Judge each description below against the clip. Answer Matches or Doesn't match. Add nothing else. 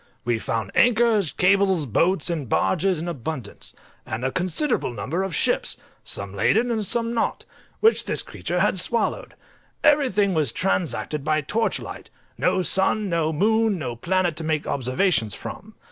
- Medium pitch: Matches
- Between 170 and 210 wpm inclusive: Doesn't match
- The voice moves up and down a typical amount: Doesn't match